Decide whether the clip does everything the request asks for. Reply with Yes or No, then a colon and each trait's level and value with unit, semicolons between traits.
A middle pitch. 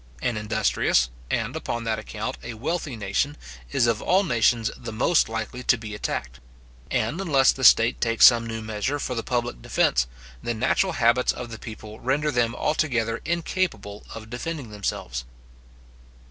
No: low, 115 Hz